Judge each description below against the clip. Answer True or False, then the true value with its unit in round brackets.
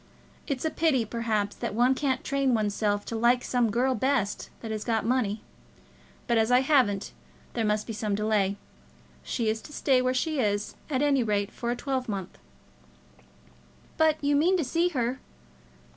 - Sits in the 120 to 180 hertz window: False (240 Hz)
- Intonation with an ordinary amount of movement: True (3.8 semitones)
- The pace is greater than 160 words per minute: True (175 wpm)